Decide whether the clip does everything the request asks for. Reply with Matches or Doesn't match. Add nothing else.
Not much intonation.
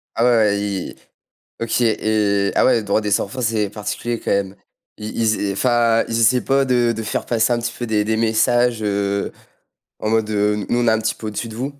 Matches